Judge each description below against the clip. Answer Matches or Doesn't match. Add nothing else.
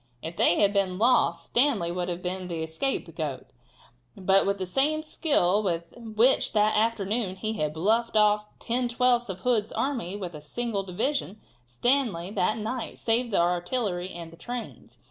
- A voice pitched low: Doesn't match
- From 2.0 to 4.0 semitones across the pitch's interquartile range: Doesn't match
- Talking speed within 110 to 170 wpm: Matches